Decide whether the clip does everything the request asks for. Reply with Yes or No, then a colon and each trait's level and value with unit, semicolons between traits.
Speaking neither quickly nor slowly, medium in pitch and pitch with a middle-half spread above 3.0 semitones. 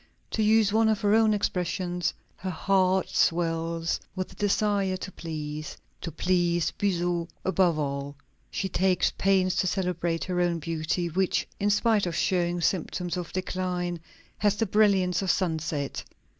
No: average, 150 wpm; medium, 180 Hz; narrow, 2.5 semitones